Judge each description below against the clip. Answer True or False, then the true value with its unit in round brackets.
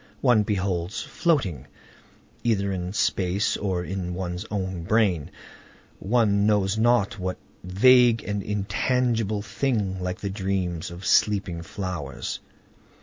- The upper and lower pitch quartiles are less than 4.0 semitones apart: True (2.9 semitones)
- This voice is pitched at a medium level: False (100 Hz)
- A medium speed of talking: False (115 wpm)